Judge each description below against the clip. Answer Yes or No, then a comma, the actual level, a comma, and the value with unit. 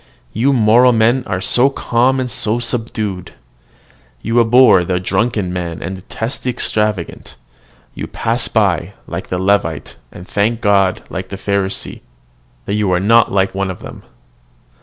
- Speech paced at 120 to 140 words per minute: No, average, 155 wpm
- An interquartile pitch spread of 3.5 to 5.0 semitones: Yes, average, 3.8 semitones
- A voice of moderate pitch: No, low, 105 Hz